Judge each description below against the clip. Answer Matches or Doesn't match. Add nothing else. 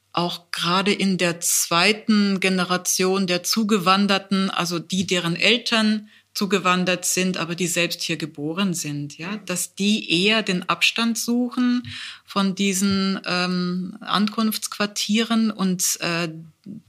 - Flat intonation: Doesn't match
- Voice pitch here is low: Doesn't match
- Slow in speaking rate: Matches